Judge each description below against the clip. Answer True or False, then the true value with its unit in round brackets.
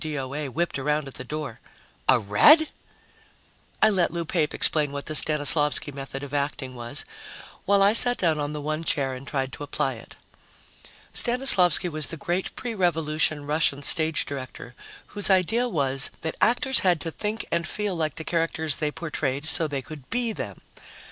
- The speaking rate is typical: True (175 wpm)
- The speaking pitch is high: False (155 Hz)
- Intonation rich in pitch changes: False (3.8 semitones)